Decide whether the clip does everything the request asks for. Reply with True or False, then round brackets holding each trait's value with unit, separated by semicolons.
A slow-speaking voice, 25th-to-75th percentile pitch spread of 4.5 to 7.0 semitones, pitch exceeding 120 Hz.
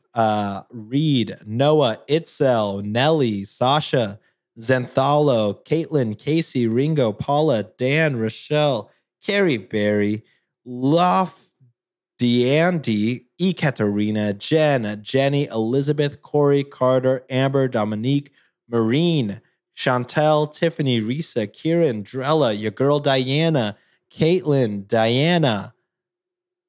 True (80 wpm; 5.1 semitones; 135 Hz)